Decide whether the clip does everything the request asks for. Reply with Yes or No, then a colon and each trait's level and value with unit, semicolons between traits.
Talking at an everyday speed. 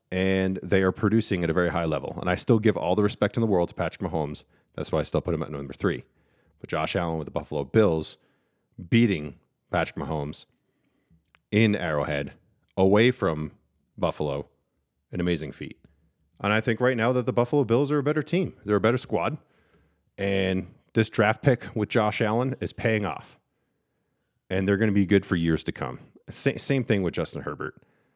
Yes: average, 195 wpm